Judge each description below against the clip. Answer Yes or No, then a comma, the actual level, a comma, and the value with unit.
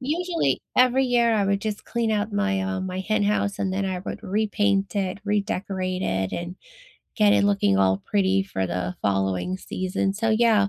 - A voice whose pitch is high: Yes, high, 200 Hz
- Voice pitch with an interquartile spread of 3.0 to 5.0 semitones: No, narrow, 2.4 semitones